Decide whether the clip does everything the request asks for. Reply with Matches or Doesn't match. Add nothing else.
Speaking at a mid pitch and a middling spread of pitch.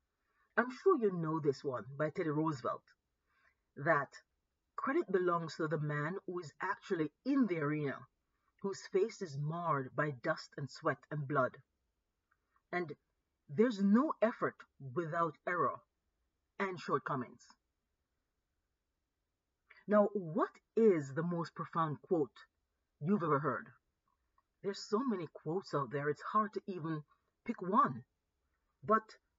Doesn't match